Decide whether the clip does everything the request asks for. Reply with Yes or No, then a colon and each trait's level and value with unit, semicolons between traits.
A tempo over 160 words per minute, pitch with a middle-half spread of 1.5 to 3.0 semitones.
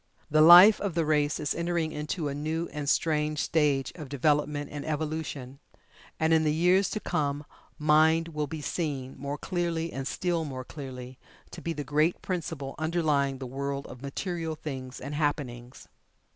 Yes: average, 170 wpm; narrow, 2.6 semitones